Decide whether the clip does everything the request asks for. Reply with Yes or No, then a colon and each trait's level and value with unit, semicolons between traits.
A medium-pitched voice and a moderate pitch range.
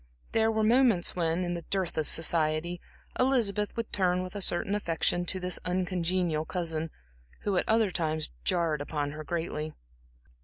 Yes: medium, 175 Hz; average, 3.4 semitones